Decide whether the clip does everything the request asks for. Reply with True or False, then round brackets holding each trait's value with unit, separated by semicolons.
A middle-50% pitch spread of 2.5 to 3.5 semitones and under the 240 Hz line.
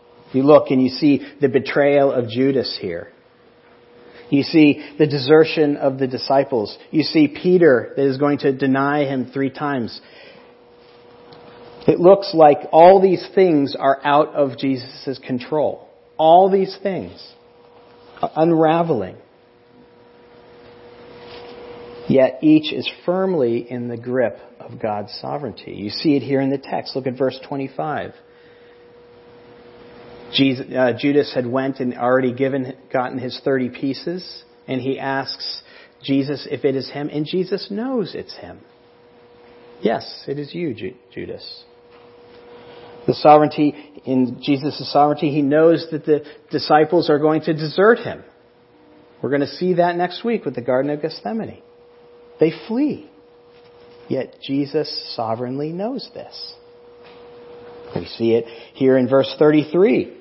False (4.0 semitones; 140 Hz)